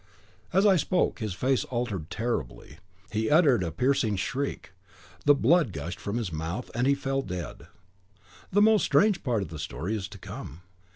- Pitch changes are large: Yes, wide, 7.2 semitones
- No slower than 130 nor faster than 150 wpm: No, average, 175 wpm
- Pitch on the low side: Yes, low, 120 Hz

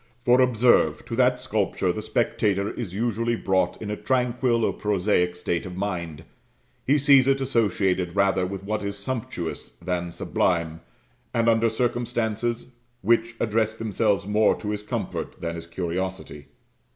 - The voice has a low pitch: Yes, low, 105 Hz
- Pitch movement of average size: Yes, average, 4.3 semitones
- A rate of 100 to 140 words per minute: No, average, 150 wpm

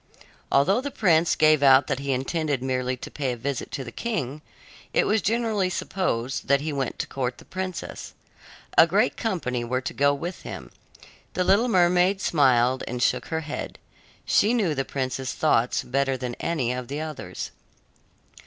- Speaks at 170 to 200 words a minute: Yes, average, 175 wpm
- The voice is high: No, medium, 140 Hz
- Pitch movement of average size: No, wide, 5.7 semitones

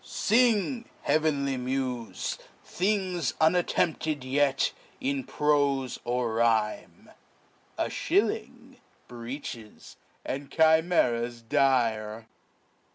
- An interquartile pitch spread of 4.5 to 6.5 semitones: Yes, average, 5.2 semitones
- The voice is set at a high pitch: No, low, 135 Hz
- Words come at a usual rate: No, slow, 70 wpm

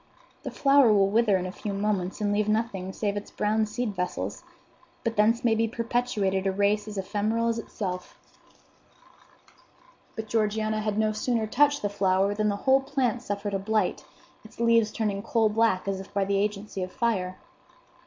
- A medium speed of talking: Yes, average, 180 wpm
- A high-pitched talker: Yes, high, 210 Hz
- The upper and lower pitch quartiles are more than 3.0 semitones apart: No, narrow, 2.4 semitones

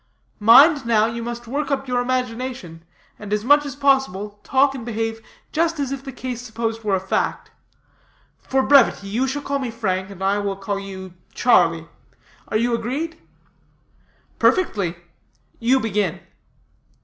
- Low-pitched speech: No, high, 235 Hz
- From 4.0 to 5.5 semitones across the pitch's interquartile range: Yes, average, 4.7 semitones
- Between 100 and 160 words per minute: Yes, average, 155 wpm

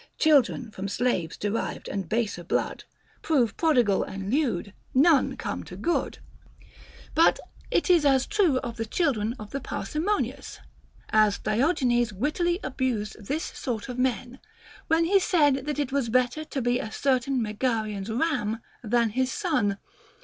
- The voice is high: Yes, very high, 250 Hz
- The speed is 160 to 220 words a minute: No, average, 150 wpm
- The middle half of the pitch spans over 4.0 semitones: Yes, average, 5.3 semitones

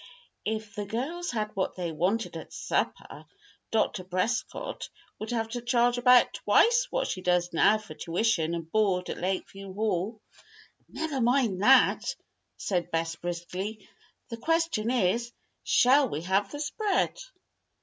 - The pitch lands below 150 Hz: No, high, 215 Hz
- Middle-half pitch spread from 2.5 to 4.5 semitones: No, average, 5.0 semitones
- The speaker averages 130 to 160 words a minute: Yes, average, 140 wpm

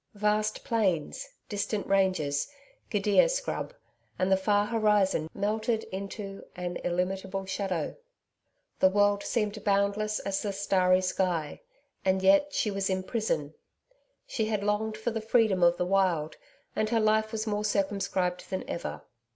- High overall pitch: Yes, high, 200 Hz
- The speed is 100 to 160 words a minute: Yes, average, 145 wpm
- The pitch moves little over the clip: Yes, narrow, 2.3 semitones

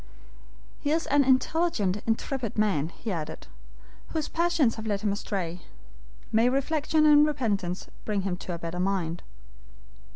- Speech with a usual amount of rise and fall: No, wide, 7.7 semitones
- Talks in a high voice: Yes, high, 215 Hz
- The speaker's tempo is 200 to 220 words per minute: No, average, 140 wpm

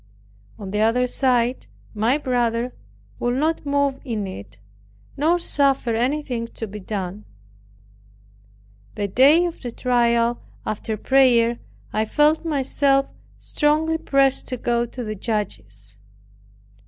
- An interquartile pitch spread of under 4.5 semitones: Yes, average, 4.0 semitones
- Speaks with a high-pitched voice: Yes, high, 245 Hz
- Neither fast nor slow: No, slow, 120 wpm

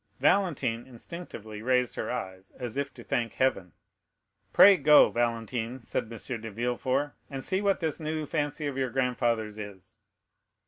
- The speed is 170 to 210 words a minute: No, average, 150 wpm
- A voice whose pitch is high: No, low, 125 Hz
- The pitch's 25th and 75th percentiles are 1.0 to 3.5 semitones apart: No, average, 4.2 semitones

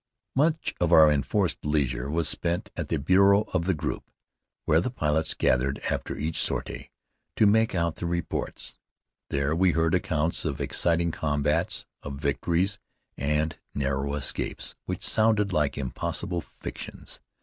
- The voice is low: Yes, very low, 80 Hz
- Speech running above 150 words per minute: No, average, 145 wpm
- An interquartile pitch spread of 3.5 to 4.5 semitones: Yes, average, 4.0 semitones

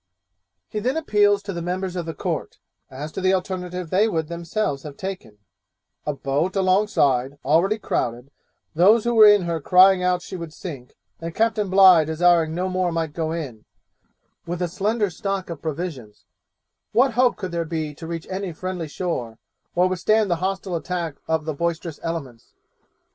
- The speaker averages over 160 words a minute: Yes, average, 175 wpm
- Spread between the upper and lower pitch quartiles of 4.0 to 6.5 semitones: No, average, 3.2 semitones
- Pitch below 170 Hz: No, medium, 175 Hz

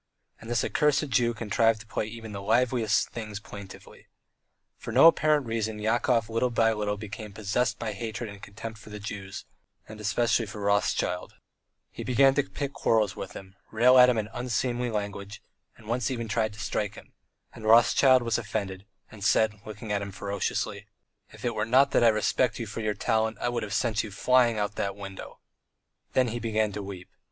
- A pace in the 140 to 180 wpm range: No, average, 195 wpm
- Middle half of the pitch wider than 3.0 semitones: No, narrow, 2.4 semitones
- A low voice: Yes, low, 110 Hz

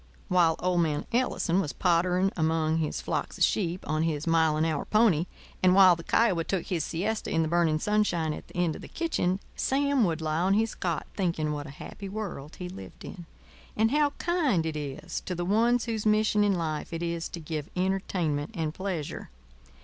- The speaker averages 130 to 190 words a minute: No, fast, 205 wpm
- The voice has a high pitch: No, medium, 175 Hz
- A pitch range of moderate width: Yes, average, 3.8 semitones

